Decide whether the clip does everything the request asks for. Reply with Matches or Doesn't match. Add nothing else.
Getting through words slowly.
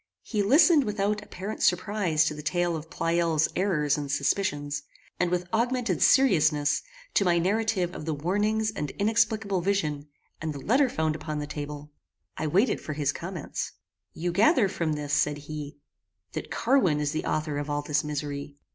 Doesn't match